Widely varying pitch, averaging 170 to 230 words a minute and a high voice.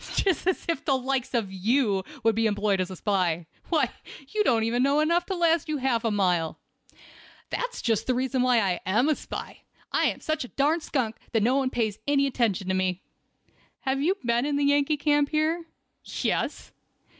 Yes: wide, 5.8 semitones; average, 190 wpm; very high, 255 Hz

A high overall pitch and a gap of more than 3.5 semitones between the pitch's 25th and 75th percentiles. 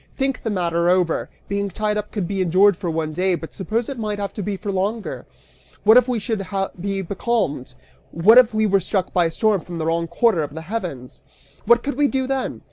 Yes: high, 200 Hz; average, 4.4 semitones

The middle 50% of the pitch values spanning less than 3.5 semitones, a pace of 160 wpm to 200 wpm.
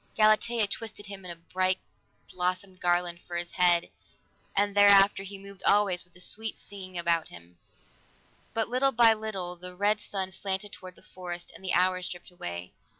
Yes: narrow, 2.4 semitones; average, 170 wpm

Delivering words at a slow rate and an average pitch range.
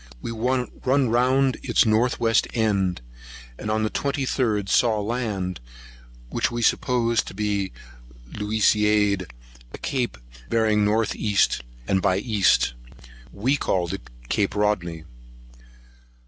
Yes: slow, 120 wpm; average, 3.1 semitones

